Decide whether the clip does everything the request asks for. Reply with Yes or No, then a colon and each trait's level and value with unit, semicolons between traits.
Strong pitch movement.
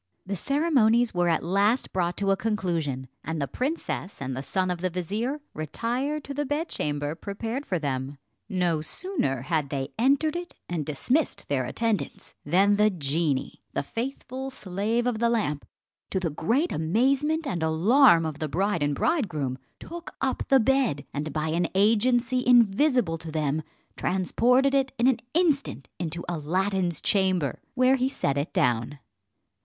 Yes: wide, 8.4 semitones